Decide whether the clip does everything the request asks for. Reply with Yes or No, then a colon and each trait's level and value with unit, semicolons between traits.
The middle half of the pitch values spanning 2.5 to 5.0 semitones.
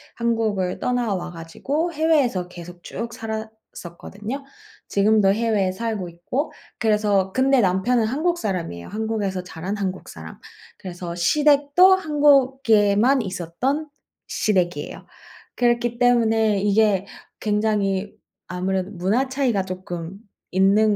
Yes: average, 4.6 semitones